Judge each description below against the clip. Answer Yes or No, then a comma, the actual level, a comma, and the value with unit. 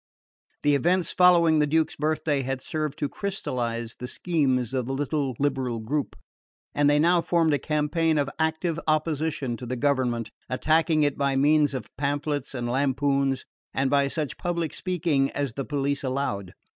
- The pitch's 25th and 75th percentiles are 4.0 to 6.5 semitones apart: No, average, 2.9 semitones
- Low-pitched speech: No, medium, 145 Hz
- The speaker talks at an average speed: Yes, average, 165 wpm